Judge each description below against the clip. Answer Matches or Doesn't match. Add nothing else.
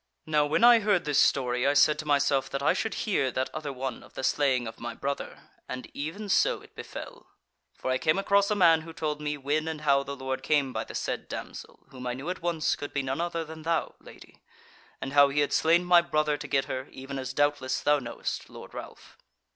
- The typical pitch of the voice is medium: Matches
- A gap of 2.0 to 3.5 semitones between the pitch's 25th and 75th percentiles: Matches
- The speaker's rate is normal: Doesn't match